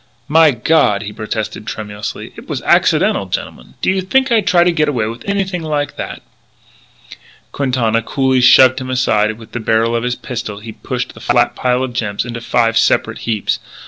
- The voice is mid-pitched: No, low, 125 Hz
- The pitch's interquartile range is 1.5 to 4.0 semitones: No, average, 4.8 semitones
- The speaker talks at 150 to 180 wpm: No, average, 195 wpm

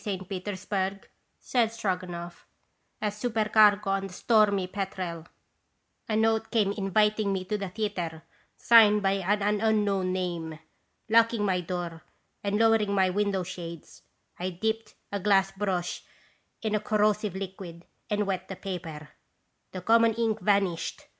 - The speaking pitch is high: Yes, high, 200 Hz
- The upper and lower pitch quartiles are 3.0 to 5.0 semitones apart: No, narrow, 2.6 semitones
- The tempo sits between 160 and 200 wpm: No, average, 140 wpm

